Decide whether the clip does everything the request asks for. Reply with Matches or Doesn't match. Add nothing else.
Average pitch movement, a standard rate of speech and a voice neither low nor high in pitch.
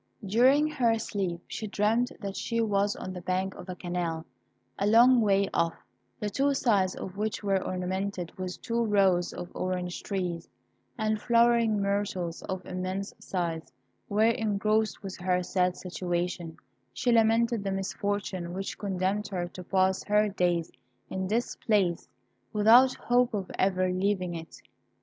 Doesn't match